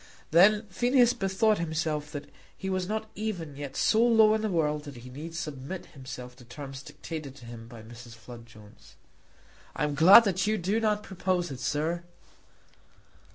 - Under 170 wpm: No, average, 175 wpm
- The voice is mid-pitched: Yes, medium, 160 Hz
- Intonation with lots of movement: Yes, wide, 6.8 semitones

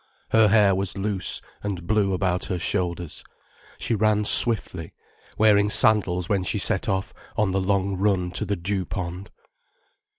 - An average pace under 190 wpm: Yes, average, 155 wpm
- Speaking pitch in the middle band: No, low, 100 Hz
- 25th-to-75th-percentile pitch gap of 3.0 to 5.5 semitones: No, narrow, 2.4 semitones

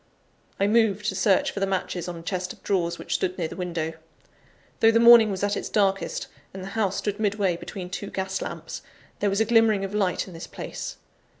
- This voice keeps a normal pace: No, fast, 220 wpm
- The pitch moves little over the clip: Yes, narrow, 2.3 semitones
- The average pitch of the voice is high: Yes, high, 195 Hz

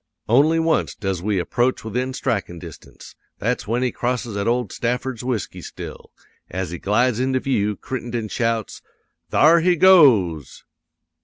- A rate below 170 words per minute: Yes, average, 145 wpm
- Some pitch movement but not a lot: Yes, average, 4.2 semitones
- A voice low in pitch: Yes, low, 120 Hz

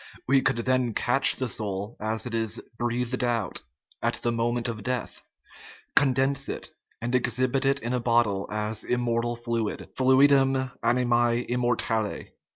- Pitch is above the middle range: No, low, 120 Hz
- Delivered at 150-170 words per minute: Yes, average, 160 wpm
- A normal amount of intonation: No, narrow, 1.9 semitones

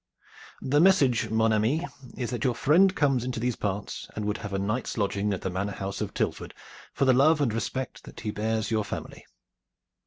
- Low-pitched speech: Yes, low, 115 Hz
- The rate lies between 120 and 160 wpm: No, fast, 205 wpm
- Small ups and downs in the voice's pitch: No, average, 4.1 semitones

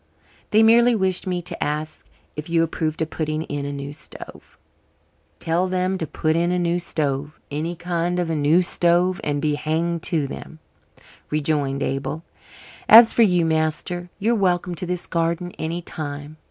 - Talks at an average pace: Yes, average, 175 wpm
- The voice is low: No, medium, 165 Hz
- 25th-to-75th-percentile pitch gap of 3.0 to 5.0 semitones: No, narrow, 2.6 semitones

